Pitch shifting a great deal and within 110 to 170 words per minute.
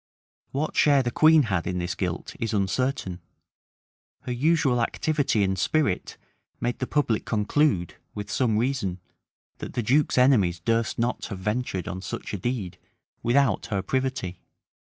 Yes: wide, 5.7 semitones; average, 150 wpm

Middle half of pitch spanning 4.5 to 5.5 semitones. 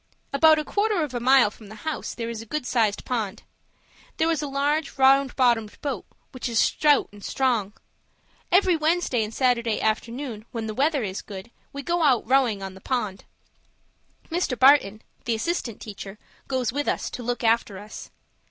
Yes: average, 4.8 semitones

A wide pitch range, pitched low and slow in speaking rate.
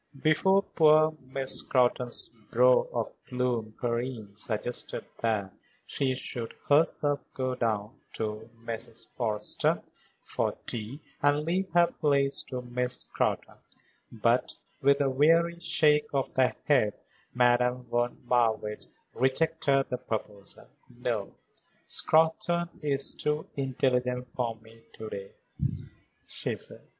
No: average, 3.7 semitones; low, 125 Hz; slow, 115 wpm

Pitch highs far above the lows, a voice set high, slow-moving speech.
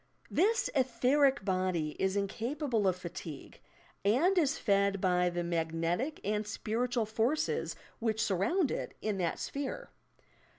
Yes: wide, 6.5 semitones; high, 215 Hz; slow, 125 wpm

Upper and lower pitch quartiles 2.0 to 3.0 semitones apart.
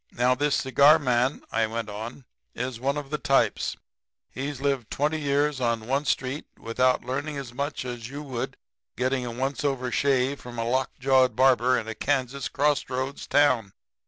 Yes: narrow, 2.5 semitones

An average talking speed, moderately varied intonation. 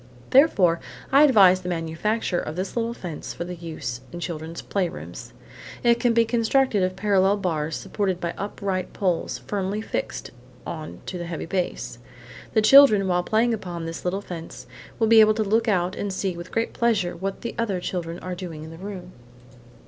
Yes: average, 180 wpm; average, 3.9 semitones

